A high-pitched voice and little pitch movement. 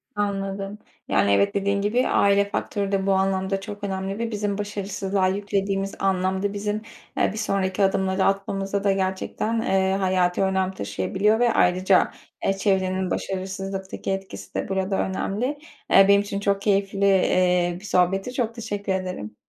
Yes: high, 195 Hz; narrow, 1.1 semitones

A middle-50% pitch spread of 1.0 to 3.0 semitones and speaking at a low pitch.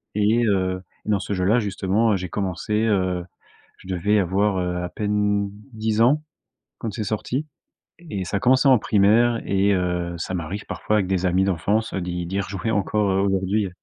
Yes: narrow, 2.5 semitones; low, 100 Hz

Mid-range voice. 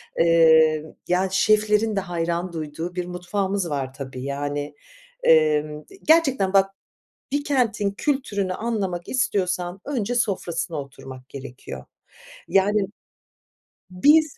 Yes: medium, 180 Hz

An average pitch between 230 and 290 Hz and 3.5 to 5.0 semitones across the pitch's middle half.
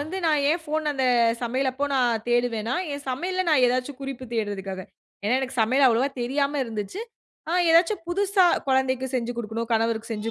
Yes: very high, 260 Hz; average, 3.9 semitones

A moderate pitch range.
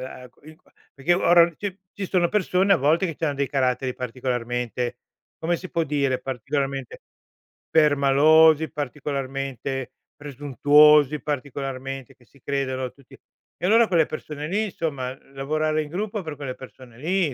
Yes: average, 3.5 semitones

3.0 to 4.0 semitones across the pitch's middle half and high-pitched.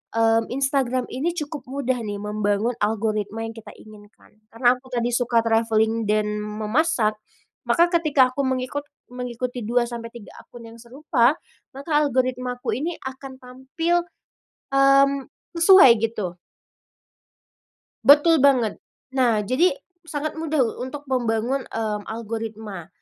Yes: average, 3.6 semitones; high, 245 Hz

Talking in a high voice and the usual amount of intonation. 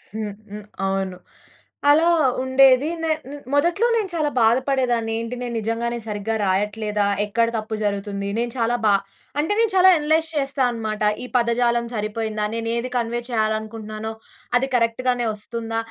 Yes: high, 230 Hz; average, 3.3 semitones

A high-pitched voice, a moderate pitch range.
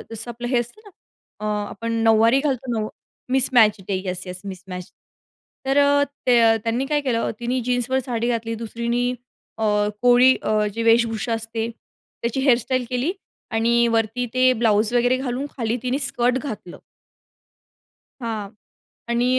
No: high, 235 Hz; narrow, 2.1 semitones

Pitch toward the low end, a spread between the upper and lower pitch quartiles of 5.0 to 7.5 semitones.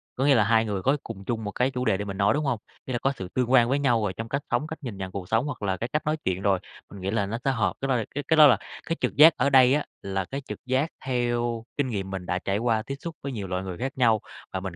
Yes: low, 120 Hz; average, 5.3 semitones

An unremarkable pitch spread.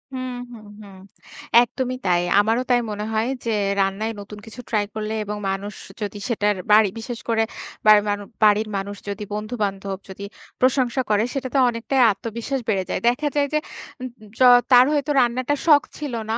Yes: average, 3.4 semitones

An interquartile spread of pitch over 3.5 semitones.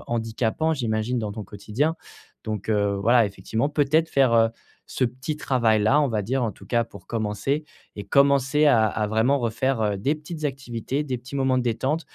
Yes: average, 4.2 semitones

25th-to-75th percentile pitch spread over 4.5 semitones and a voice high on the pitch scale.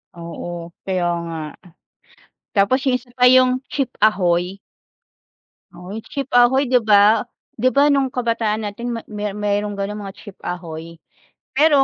Yes: average, 5.2 semitones; high, 210 Hz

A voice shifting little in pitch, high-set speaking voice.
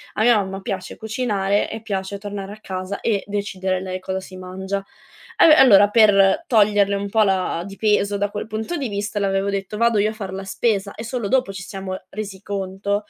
Yes: narrow, 1.8 semitones; high, 200 Hz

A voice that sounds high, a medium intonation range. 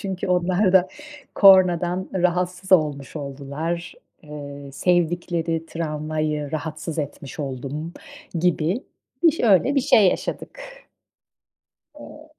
No: medium, 170 Hz; average, 3.3 semitones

